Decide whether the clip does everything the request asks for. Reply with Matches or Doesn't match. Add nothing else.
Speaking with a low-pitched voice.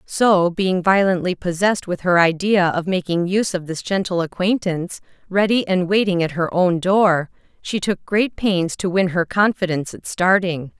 Doesn't match